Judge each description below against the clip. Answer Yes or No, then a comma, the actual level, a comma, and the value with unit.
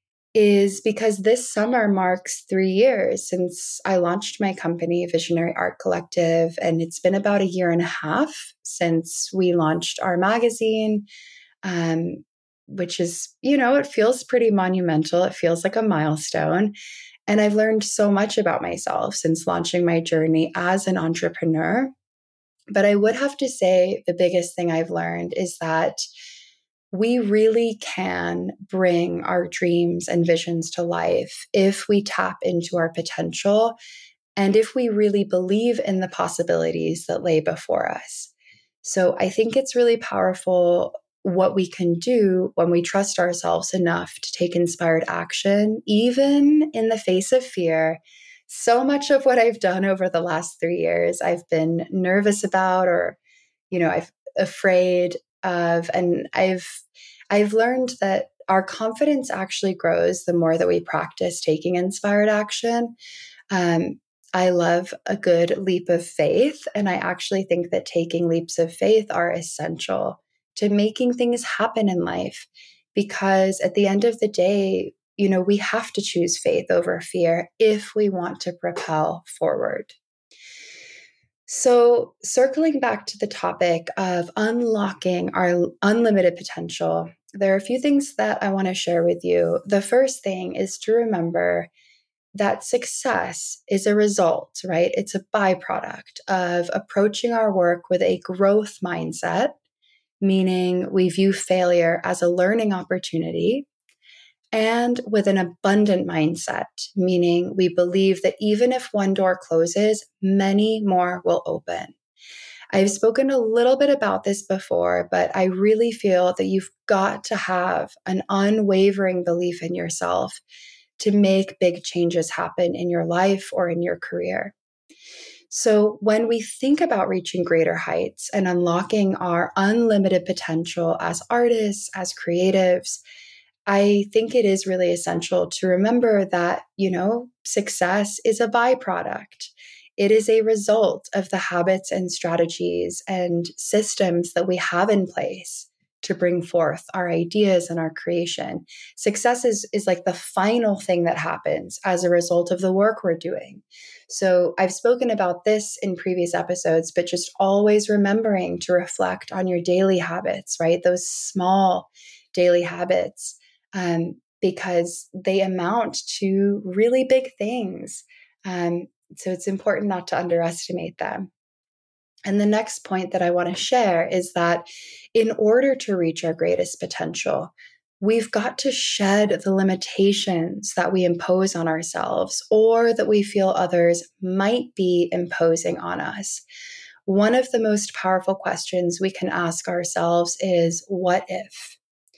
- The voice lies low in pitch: No, high, 190 Hz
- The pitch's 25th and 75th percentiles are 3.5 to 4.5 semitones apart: Yes, average, 3.8 semitones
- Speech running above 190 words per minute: No, average, 150 wpm